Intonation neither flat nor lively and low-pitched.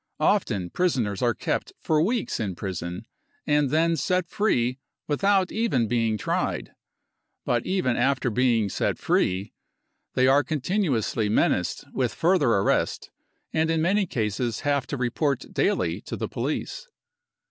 No: wide, 6.6 semitones; low, 130 Hz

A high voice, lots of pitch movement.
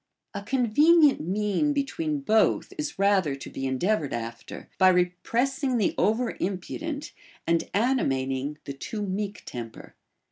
Yes: high, 205 Hz; wide, 8.2 semitones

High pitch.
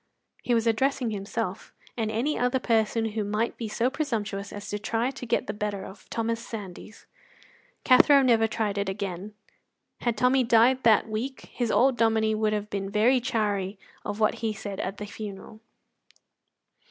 Yes: high, 220 Hz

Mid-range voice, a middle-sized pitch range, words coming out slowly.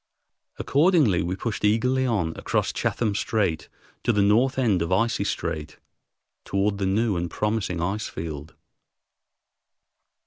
No: low, 100 Hz; average, 4.7 semitones; slow, 130 wpm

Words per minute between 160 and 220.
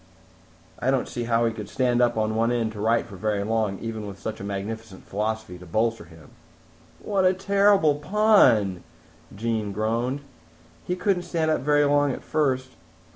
Yes: average, 180 wpm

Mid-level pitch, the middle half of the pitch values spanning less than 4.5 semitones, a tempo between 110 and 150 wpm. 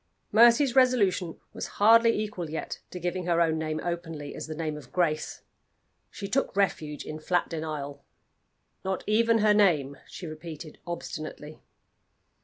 No: medium, 170 Hz; average, 5.0 semitones; average, 145 wpm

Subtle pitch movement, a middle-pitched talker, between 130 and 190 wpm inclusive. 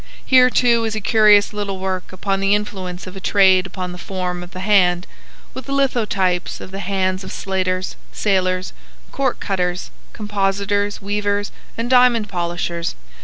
No: narrow, 2.2 semitones; high, 195 Hz; average, 150 wpm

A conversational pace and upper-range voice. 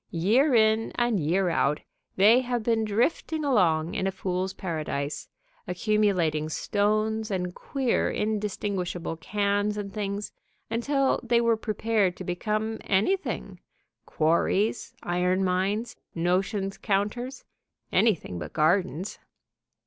No: slow, 110 wpm; high, 205 Hz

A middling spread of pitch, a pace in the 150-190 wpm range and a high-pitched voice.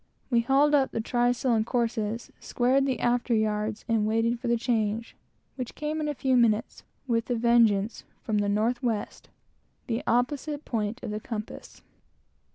No: narrow, 2.3 semitones; average, 165 wpm; high, 235 Hz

